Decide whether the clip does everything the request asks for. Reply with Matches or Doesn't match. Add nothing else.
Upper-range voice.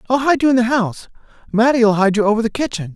Matches